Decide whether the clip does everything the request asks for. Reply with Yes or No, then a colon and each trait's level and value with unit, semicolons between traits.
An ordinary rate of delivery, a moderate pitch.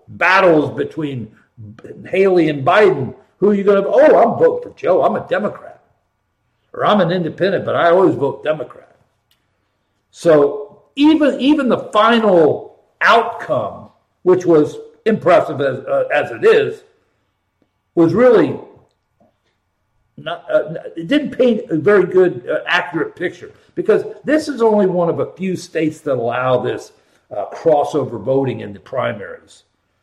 Yes: average, 145 wpm; medium, 180 Hz